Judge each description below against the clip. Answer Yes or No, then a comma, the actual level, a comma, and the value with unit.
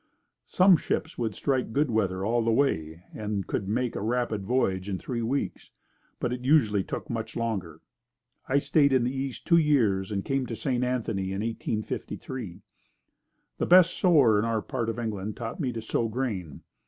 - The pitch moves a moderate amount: Yes, average, 4.1 semitones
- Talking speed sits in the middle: Yes, average, 185 wpm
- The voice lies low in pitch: Yes, low, 115 Hz